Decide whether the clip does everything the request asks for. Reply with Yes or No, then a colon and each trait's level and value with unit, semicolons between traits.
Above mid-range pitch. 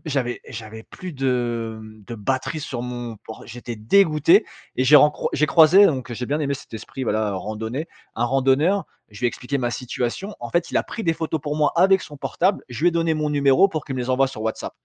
No: low, 135 Hz